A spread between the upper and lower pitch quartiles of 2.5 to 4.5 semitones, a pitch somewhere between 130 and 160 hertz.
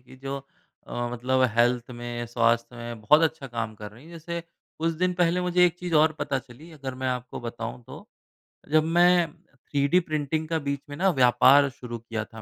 No: average, 5.2 semitones; low, 135 Hz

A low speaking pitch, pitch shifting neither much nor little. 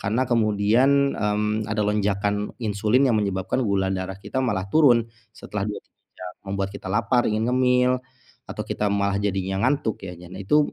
Yes: low, 105 Hz; average, 3.7 semitones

